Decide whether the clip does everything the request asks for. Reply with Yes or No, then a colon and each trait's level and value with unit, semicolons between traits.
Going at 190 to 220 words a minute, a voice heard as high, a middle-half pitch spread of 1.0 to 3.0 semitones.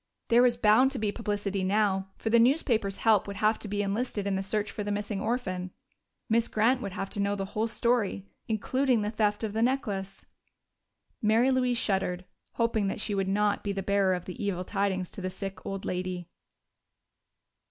Yes: average, 195 wpm; high, 205 Hz; narrow, 2.6 semitones